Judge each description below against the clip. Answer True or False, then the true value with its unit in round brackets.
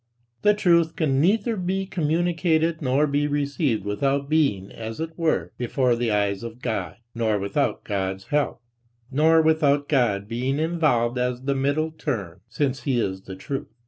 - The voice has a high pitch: False (140 Hz)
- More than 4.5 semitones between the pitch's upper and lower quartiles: True (5.5 semitones)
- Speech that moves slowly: False (160 wpm)